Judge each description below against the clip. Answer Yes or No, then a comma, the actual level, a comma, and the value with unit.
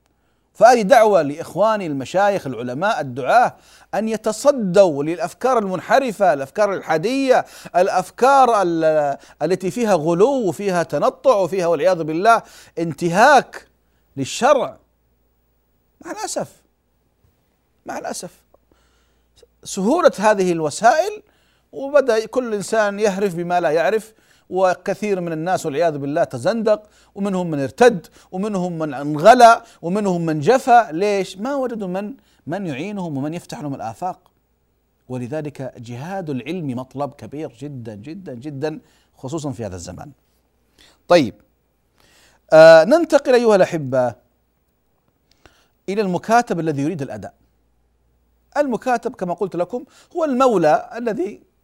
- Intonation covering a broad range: Yes, wide, 8.0 semitones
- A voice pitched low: No, medium, 175 Hz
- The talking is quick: No, average, 105 wpm